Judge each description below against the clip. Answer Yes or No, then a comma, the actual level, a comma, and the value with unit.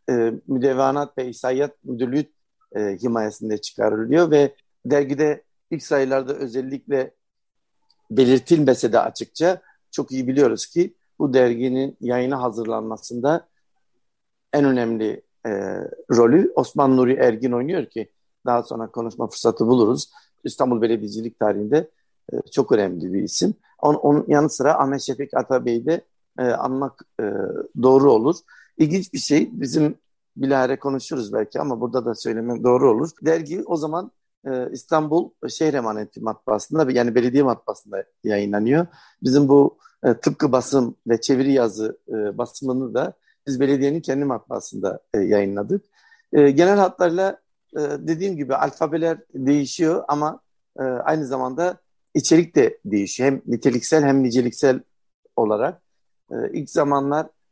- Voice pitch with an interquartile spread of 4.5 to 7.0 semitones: No, average, 3.8 semitones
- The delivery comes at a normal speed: Yes, average, 125 wpm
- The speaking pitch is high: No, low, 135 Hz